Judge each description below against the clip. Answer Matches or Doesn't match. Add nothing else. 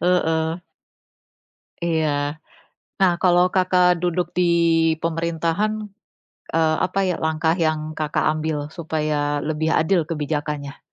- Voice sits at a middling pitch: Matches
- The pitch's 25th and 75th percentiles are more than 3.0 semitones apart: Doesn't match